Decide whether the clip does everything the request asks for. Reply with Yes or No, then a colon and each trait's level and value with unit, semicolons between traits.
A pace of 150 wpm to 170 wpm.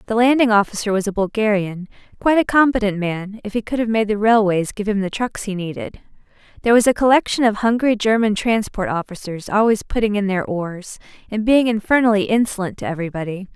No: average, 190 wpm